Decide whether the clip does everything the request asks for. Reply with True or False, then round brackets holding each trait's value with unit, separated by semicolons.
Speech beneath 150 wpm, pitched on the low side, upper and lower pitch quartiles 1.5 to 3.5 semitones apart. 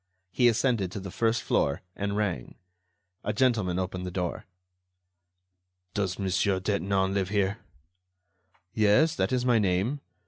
True (135 wpm; 100 Hz; 3.2 semitones)